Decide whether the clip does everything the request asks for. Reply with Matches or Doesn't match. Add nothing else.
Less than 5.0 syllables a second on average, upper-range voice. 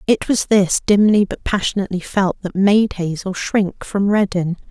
Matches